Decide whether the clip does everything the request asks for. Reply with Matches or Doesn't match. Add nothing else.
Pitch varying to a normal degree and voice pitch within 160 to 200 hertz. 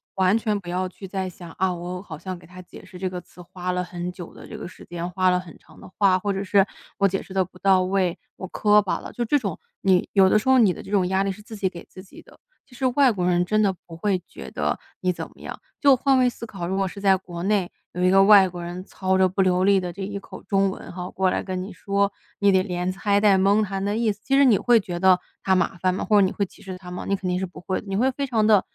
Doesn't match